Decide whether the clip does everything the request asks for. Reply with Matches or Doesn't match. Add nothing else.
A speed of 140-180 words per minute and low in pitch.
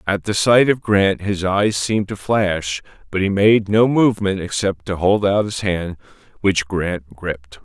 Doesn't match